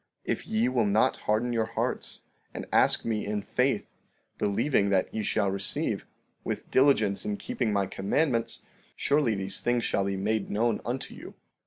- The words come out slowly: No, average, 165 wpm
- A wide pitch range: No, average, 3.1 semitones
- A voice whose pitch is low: Yes, low, 110 Hz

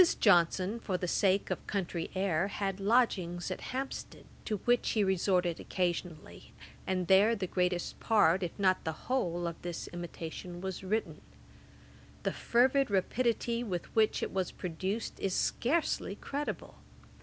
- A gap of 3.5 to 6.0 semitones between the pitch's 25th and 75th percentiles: Yes, average, 3.9 semitones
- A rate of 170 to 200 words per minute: No, average, 145 wpm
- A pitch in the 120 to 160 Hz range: No, high, 190 Hz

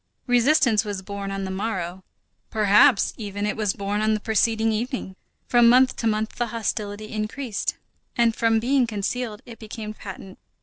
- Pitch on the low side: No, high, 215 Hz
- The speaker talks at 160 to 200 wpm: Yes, average, 165 wpm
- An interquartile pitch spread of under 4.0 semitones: Yes, narrow, 2.5 semitones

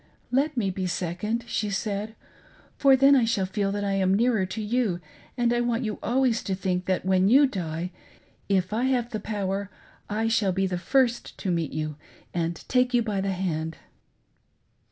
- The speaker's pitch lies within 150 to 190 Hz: No, high, 205 Hz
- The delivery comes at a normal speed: Yes, average, 190 wpm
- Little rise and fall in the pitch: No, average, 4.2 semitones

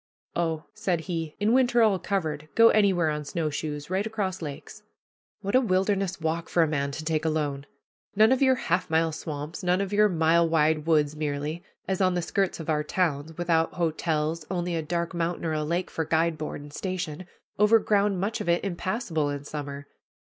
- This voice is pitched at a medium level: Yes, medium, 165 Hz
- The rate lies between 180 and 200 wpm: Yes, average, 195 wpm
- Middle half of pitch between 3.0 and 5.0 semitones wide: Yes, average, 3.6 semitones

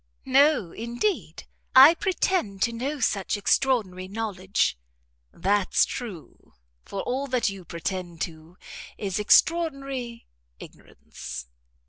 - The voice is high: Yes, high, 220 Hz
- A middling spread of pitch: No, wide, 6.3 semitones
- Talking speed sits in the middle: No, slow, 100 wpm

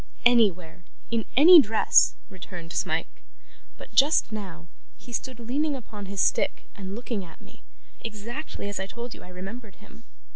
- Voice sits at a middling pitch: No, high, 215 Hz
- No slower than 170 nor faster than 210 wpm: No, average, 155 wpm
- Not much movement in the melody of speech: No, average, 4.0 semitones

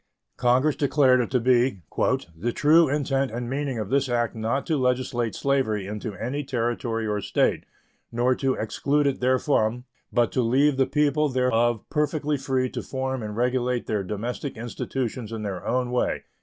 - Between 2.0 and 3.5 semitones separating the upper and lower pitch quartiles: Yes, average, 2.9 semitones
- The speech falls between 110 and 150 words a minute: No, average, 170 wpm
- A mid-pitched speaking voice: No, low, 125 Hz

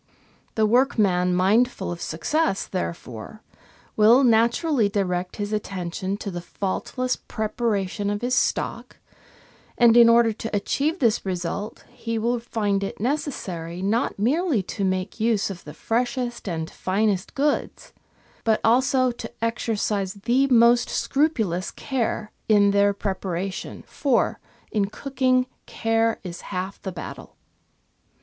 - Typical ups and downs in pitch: Yes, average, 3.9 semitones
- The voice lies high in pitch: Yes, high, 215 Hz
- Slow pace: Yes, slow, 130 wpm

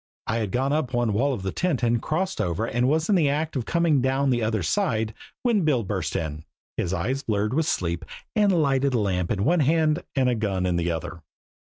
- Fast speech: Yes, fast, 230 wpm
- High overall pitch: No, low, 125 Hz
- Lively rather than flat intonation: Yes, wide, 6.9 semitones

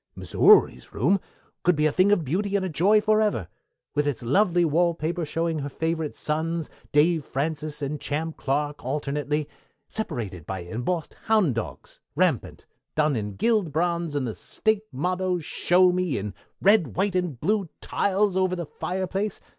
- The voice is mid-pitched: Yes, medium, 165 Hz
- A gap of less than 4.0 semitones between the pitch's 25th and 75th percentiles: No, average, 4.3 semitones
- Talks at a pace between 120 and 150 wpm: No, average, 160 wpm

